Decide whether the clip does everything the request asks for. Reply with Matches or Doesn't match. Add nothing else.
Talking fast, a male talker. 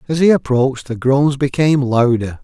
Doesn't match